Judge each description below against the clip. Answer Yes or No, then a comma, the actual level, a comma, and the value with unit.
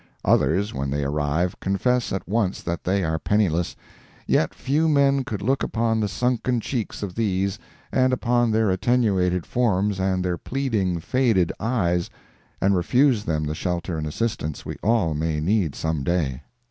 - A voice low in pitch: Yes, very low, 95 Hz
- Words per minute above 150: Yes, average, 160 wpm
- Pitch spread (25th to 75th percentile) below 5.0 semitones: No, wide, 5.4 semitones